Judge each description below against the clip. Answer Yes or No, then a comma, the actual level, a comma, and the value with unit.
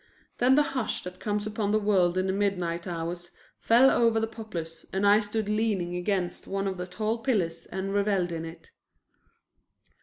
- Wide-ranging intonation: No, average, 3.5 semitones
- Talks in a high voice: Yes, high, 195 Hz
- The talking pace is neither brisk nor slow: Yes, average, 180 wpm